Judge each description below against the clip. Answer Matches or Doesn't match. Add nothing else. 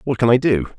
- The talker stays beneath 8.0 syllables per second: Matches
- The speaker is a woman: Doesn't match